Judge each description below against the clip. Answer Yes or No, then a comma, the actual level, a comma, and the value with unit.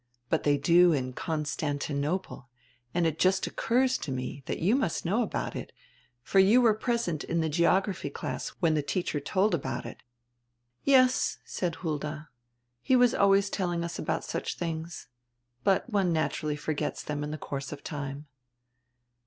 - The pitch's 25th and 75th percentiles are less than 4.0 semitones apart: No, average, 4.7 semitones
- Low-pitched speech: No, medium, 170 Hz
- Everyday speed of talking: Yes, average, 160 wpm